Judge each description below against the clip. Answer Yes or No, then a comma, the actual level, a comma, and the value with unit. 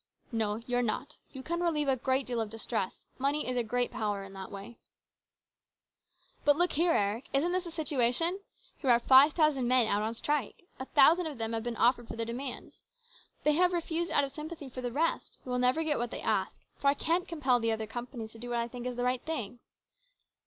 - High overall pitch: Yes, very high, 255 Hz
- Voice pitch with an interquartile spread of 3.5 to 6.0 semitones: Yes, average, 4.5 semitones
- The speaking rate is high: Yes, fast, 230 wpm